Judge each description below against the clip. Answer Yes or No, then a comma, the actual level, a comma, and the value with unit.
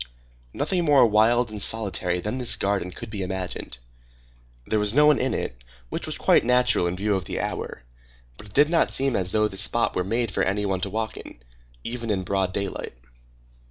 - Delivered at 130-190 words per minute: No, fast, 205 wpm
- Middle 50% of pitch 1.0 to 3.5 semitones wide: No, average, 4.0 semitones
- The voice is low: Yes, low, 105 Hz